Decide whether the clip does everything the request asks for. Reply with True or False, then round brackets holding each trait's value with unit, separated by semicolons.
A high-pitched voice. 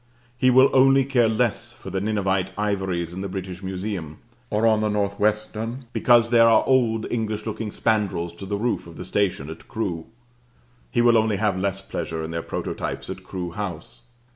False (105 Hz)